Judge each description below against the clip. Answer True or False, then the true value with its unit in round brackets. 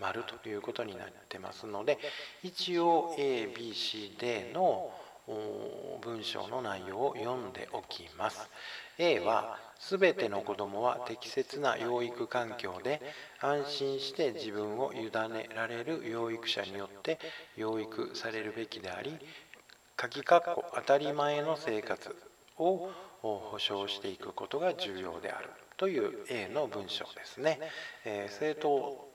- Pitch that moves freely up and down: True (6.8 semitones)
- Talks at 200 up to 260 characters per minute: True (245 characters per minute)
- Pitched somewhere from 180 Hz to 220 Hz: False (135 Hz)